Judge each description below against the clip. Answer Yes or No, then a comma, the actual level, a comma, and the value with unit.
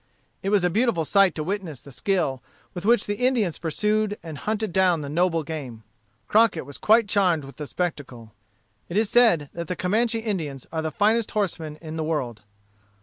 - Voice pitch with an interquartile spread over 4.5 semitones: Yes, wide, 5.5 semitones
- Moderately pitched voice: Yes, medium, 175 Hz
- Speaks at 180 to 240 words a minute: Yes, average, 190 wpm